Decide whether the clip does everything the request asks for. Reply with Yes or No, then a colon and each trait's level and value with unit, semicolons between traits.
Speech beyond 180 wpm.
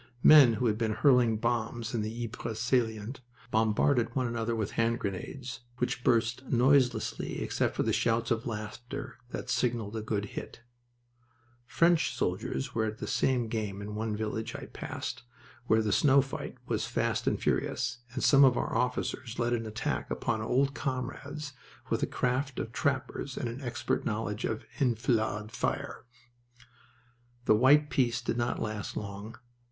No: average, 160 wpm